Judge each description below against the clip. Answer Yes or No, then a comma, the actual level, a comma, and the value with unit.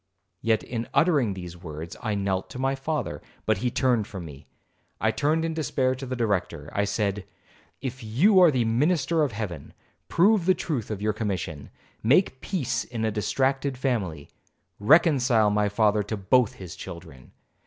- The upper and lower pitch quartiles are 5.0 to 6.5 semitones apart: Yes, average, 5.3 semitones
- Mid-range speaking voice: No, low, 115 Hz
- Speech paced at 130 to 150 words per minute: No, average, 165 wpm